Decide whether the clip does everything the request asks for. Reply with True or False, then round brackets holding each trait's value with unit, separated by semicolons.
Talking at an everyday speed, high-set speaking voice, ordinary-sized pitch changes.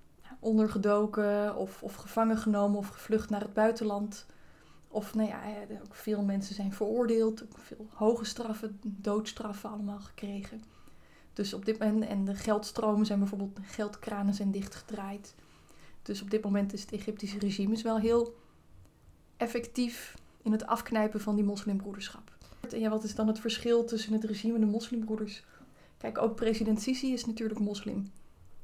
False (155 wpm; 215 Hz; 1.5 semitones)